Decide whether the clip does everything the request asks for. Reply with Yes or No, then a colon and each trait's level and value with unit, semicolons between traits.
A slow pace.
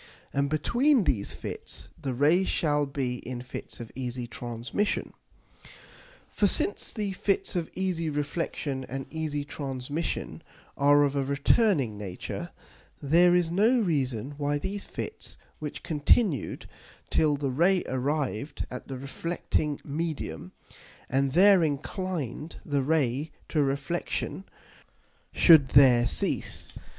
Yes: slow, 120 wpm